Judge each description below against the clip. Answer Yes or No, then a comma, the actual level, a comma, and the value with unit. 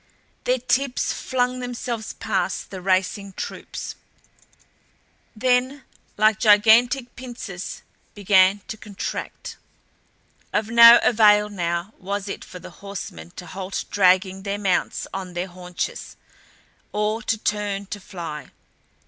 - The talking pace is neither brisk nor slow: No, slow, 115 wpm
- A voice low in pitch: No, high, 205 Hz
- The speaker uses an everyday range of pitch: Yes, average, 3.6 semitones